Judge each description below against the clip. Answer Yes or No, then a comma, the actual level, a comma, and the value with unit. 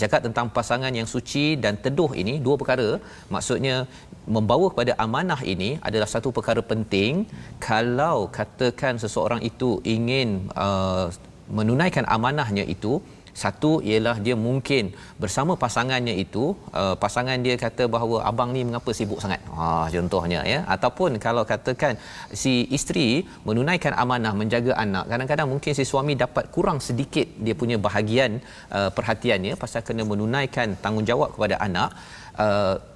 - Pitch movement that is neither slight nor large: Yes, average, 3.5 semitones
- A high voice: No, low, 120 Hz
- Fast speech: Yes, fast, 140 wpm